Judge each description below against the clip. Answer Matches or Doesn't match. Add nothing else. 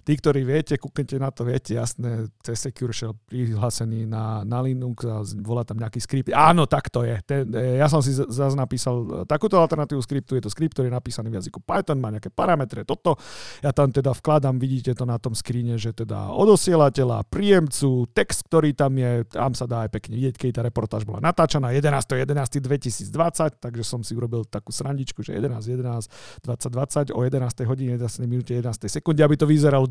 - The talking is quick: Matches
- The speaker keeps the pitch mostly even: Doesn't match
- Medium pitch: Doesn't match